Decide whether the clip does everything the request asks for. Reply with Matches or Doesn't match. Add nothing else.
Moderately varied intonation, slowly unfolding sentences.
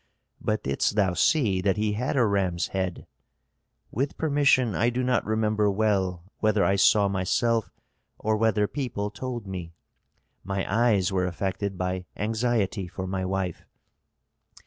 Doesn't match